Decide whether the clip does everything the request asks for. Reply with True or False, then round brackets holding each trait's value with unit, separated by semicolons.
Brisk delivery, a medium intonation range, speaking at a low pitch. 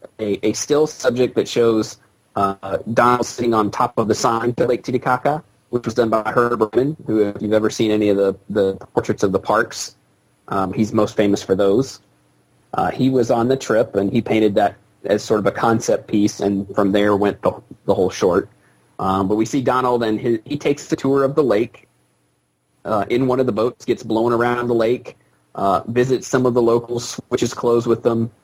True (210 wpm; 3.3 semitones; 115 Hz)